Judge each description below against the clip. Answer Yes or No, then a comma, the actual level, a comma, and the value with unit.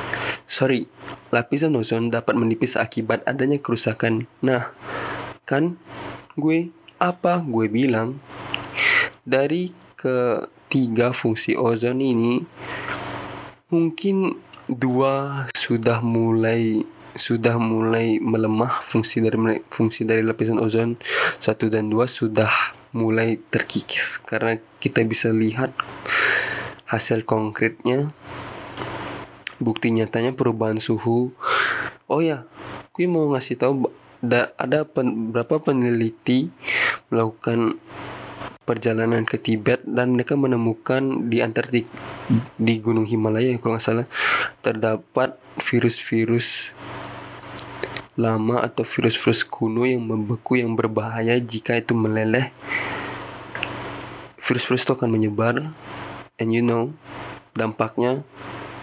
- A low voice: Yes, low, 115 Hz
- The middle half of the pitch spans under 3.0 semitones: Yes, narrow, 2.5 semitones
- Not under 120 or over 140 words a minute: No, average, 95 wpm